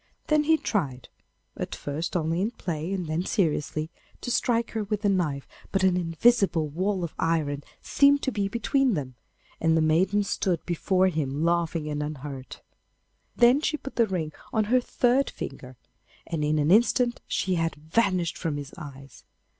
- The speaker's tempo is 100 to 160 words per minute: No, average, 170 wpm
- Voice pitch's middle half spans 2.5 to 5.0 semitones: No, wide, 5.5 semitones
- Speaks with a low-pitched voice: No, medium, 175 Hz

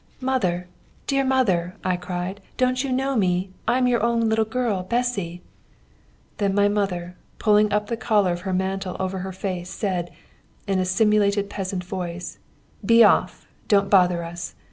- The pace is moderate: Yes, average, 165 wpm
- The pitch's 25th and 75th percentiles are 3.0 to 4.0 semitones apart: Yes, average, 3.7 semitones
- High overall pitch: Yes, high, 195 Hz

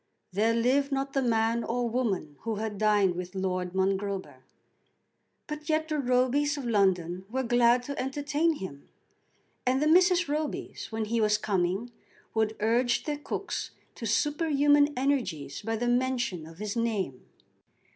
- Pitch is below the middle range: No, high, 235 Hz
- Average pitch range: No, wide, 5.7 semitones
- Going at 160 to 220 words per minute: No, average, 150 wpm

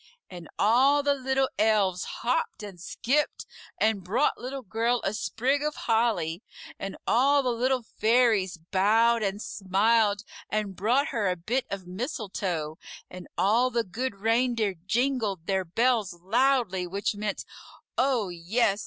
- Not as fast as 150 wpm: Yes, average, 140 wpm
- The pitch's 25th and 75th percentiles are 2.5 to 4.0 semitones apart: No, average, 4.5 semitones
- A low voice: No, high, 220 Hz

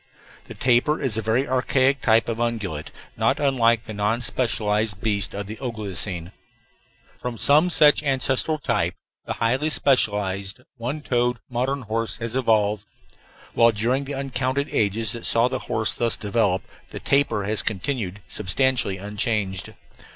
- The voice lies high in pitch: No, low, 115 Hz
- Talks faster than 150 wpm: No, average, 145 wpm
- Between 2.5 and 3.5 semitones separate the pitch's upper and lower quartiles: No, average, 3.9 semitones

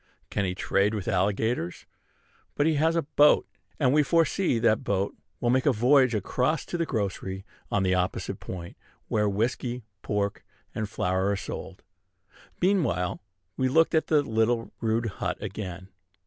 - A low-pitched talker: Yes, low, 110 Hz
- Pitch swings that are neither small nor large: No, wide, 6.1 semitones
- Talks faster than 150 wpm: Yes, average, 160 wpm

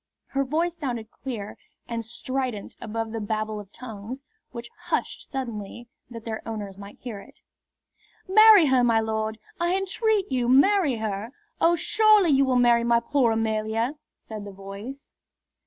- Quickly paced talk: No, average, 155 wpm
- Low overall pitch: No, high, 235 Hz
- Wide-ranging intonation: No, average, 4.1 semitones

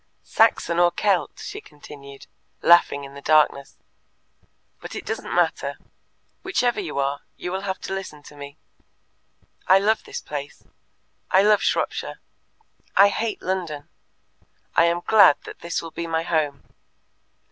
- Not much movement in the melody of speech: No, average, 4.9 semitones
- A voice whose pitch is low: No, medium, 170 Hz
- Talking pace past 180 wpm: No, average, 145 wpm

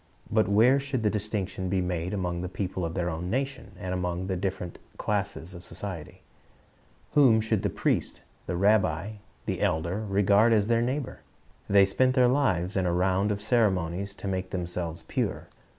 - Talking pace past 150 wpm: Yes, average, 170 wpm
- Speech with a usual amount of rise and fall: Yes, average, 3.3 semitones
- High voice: No, very low, 95 Hz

